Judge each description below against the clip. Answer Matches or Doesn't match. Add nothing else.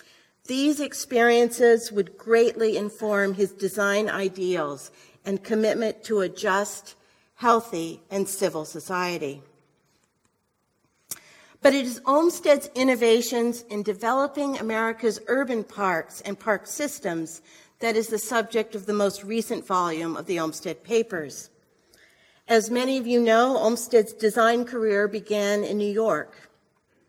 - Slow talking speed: Matches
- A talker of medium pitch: Doesn't match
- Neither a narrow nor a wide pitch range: Matches